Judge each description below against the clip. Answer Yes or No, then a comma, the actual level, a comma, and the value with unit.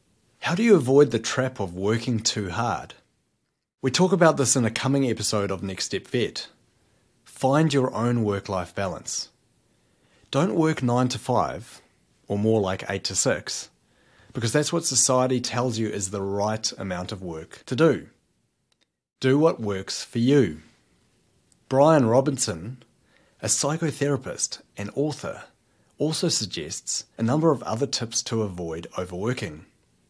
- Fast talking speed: No, average, 150 wpm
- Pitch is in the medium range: No, low, 120 Hz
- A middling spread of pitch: Yes, average, 4.9 semitones